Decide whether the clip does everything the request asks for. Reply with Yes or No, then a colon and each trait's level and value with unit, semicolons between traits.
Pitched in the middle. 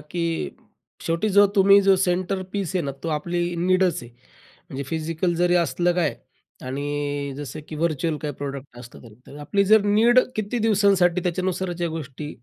Yes: medium, 175 Hz